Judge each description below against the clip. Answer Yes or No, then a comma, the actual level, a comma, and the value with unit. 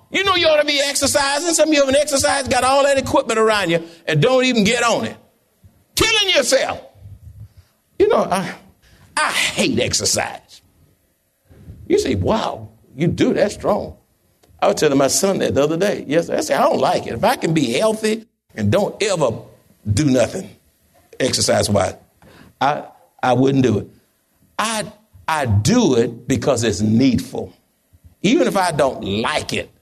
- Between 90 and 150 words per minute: No, average, 170 wpm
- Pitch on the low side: No, high, 215 Hz